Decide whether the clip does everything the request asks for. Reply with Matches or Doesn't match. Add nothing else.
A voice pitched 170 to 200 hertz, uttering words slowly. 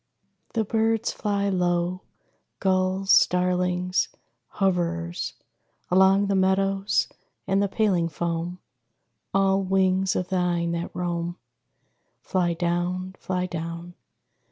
Matches